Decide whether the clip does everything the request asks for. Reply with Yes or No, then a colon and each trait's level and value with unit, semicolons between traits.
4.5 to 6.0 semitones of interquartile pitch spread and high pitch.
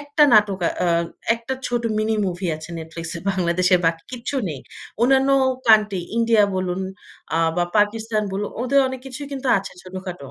Yes: average, 5.0 semitones; high, 205 Hz